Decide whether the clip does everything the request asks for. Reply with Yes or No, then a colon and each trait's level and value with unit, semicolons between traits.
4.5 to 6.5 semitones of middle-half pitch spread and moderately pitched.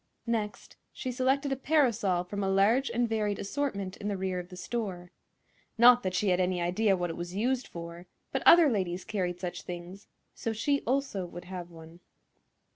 No: average, 5.0 semitones; high, 195 Hz